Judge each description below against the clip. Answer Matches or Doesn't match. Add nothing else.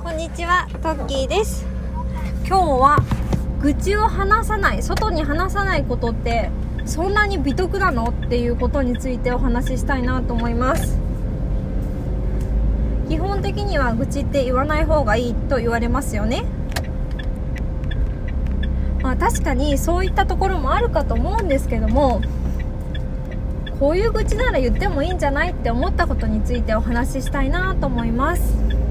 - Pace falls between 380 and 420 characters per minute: Doesn't match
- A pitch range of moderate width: Doesn't match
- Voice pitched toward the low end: Matches